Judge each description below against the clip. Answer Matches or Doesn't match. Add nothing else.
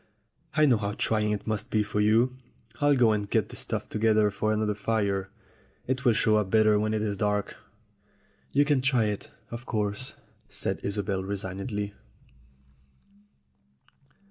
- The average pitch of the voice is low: Matches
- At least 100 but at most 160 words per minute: Matches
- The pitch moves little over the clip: Matches